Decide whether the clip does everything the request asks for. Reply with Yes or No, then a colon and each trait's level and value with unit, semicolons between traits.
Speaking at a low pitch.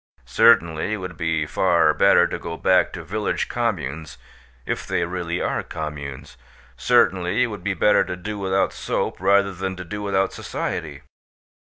Yes: very low, 90 Hz